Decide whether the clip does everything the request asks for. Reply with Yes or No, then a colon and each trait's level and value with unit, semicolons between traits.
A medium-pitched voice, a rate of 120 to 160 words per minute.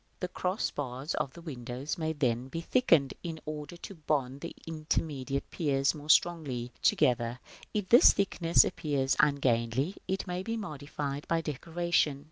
Yes: medium, 150 Hz; average, 155 wpm